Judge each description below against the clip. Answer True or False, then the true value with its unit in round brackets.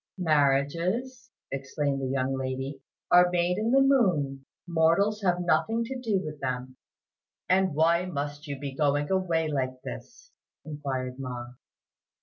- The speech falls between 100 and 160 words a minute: True (135 wpm)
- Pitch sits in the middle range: True (150 Hz)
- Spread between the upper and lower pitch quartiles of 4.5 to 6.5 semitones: True (5.2 semitones)